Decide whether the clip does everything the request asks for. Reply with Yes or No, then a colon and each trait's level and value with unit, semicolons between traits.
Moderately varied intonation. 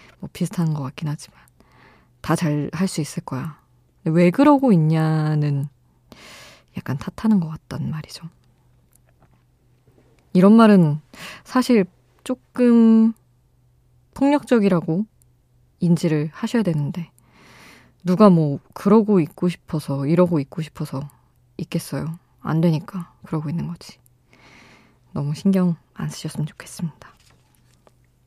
No: wide, 5.7 semitones